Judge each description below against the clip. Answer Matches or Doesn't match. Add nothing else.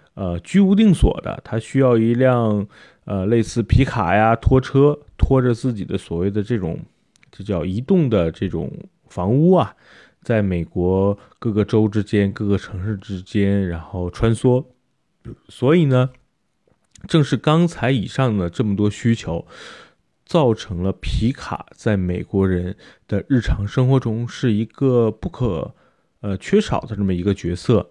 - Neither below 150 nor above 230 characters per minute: Matches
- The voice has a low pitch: Matches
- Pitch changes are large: Doesn't match